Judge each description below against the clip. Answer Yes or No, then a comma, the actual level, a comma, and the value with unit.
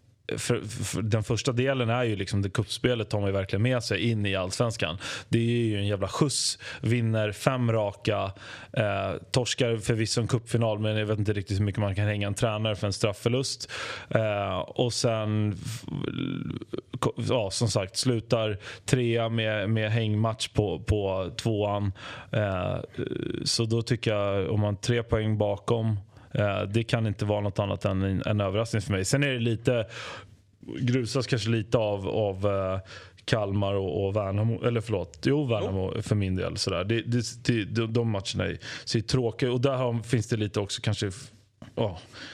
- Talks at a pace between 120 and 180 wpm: Yes, average, 165 wpm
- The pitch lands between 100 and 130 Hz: Yes, low, 110 Hz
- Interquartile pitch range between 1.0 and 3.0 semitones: Yes, narrow, 2.6 semitones